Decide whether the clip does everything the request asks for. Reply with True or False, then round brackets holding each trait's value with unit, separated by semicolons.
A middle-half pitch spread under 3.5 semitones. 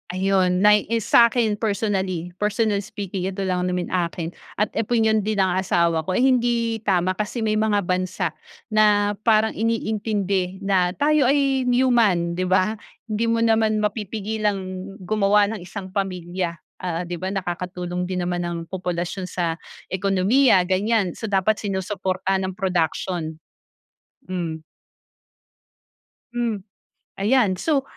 True (3.1 semitones)